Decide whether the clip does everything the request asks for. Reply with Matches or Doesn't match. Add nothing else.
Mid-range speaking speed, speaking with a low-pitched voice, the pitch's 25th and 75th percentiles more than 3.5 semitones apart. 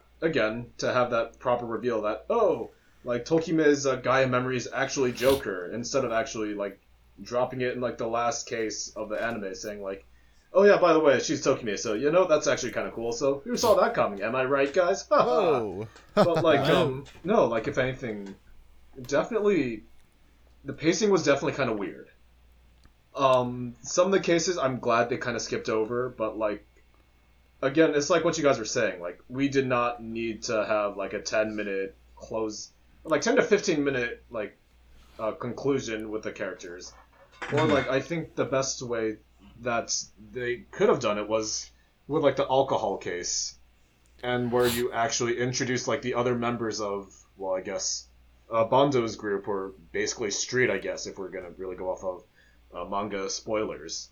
Matches